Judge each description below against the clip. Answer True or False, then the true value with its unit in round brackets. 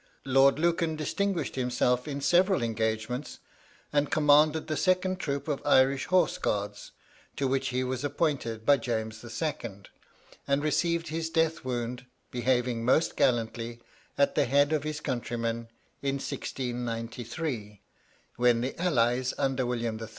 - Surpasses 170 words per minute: False (135 wpm)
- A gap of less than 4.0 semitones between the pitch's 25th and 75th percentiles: False (4.3 semitones)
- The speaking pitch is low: True (130 Hz)